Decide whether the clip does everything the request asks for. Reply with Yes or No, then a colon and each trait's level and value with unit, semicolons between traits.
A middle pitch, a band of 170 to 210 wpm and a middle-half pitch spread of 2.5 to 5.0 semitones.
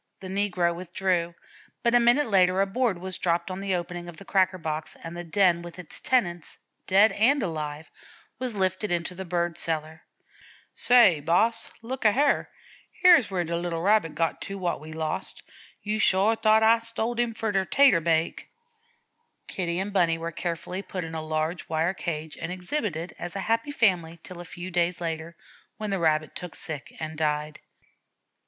Yes: medium, 180 Hz; average, 185 wpm; average, 3.7 semitones